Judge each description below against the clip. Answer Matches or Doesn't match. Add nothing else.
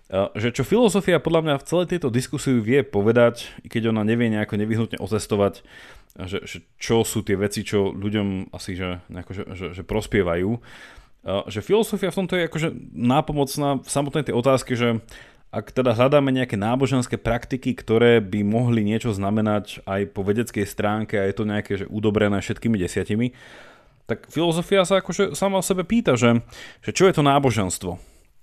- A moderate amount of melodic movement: Matches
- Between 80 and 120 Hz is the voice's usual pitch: Matches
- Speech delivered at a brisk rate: Matches